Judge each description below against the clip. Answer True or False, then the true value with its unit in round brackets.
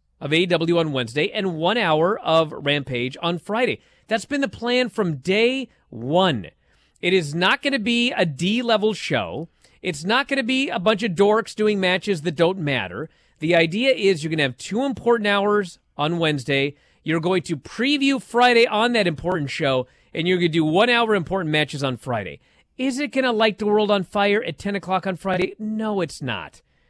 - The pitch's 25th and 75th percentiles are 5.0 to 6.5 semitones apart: True (5.6 semitones)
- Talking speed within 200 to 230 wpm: True (205 wpm)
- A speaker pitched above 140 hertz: True (185 Hz)